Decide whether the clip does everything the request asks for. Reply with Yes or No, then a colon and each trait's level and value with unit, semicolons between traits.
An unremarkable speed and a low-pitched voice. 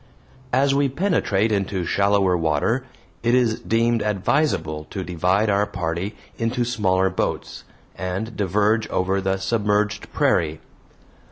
No: slow, 120 wpm; low, 100 Hz